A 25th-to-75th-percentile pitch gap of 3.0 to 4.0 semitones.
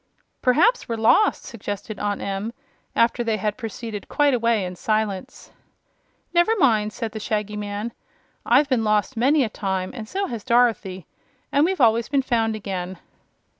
Yes: average, 3.4 semitones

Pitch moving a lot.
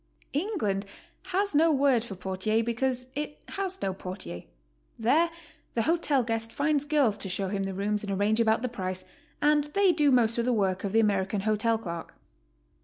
Yes: wide, 6.5 semitones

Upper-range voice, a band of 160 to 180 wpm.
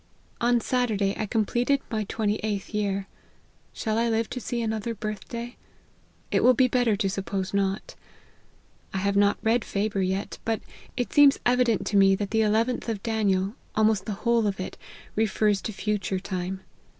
Yes: high, 215 Hz; average, 175 wpm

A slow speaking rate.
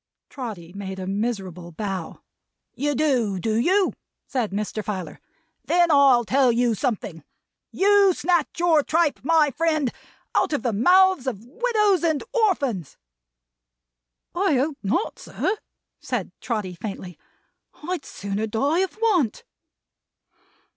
Yes: slow, 125 wpm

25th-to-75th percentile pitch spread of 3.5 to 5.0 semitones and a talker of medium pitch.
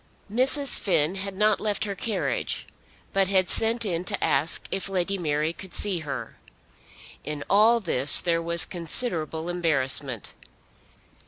Yes: average, 4.2 semitones; medium, 180 Hz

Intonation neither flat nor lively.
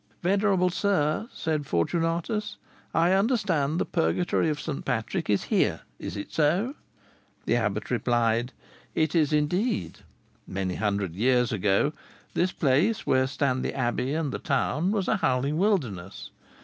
No: wide, 7.0 semitones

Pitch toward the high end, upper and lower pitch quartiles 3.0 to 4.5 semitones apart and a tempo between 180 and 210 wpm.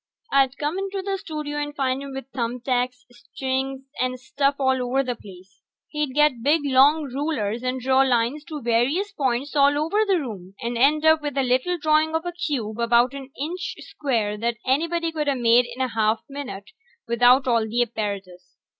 Yes: very high, 265 Hz; average, 3.9 semitones; average, 195 wpm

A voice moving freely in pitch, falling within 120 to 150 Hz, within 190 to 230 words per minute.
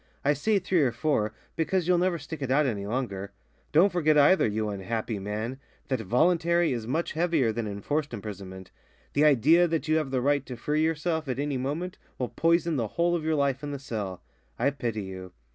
Yes: wide, 6.2 semitones; medium, 140 Hz; fast, 205 wpm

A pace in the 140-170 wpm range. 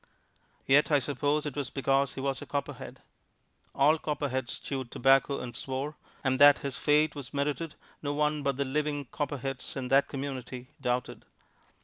Yes: average, 160 wpm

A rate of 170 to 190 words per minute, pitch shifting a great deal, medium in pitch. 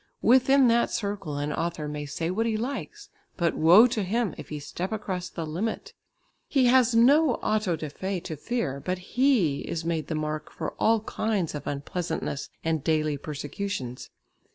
Yes: average, 175 wpm; wide, 6.9 semitones; medium, 180 Hz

